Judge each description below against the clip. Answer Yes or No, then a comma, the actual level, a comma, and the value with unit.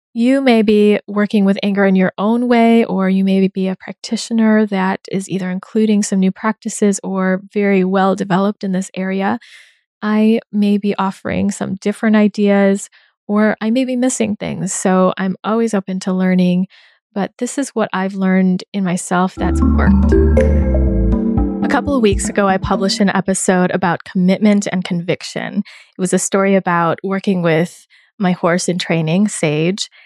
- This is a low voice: No, high, 195 Hz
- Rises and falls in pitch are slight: Yes, narrow, 2.1 semitones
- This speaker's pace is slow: No, average, 170 wpm